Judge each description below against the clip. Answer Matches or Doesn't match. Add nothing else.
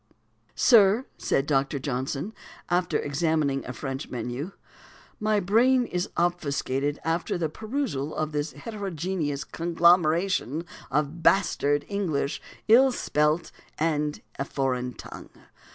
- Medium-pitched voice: Matches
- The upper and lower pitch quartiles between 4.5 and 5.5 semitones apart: Matches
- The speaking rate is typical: Doesn't match